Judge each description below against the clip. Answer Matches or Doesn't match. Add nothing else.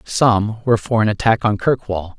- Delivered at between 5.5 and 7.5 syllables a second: Doesn't match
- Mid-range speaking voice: Doesn't match